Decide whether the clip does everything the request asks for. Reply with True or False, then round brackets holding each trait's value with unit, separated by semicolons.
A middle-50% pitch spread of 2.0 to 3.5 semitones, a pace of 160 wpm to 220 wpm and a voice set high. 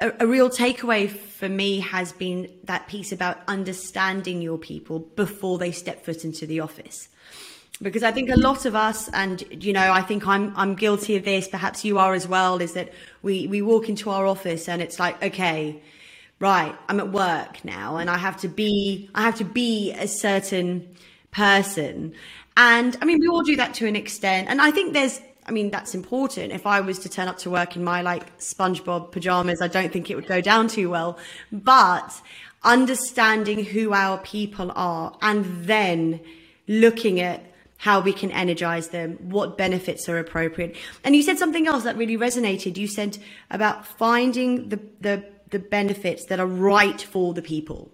True (3.2 semitones; 190 wpm; 195 Hz)